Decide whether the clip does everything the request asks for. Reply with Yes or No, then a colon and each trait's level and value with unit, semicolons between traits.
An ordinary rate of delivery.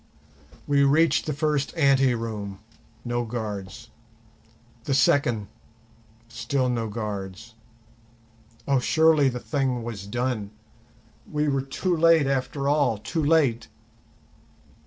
No: slow, 105 wpm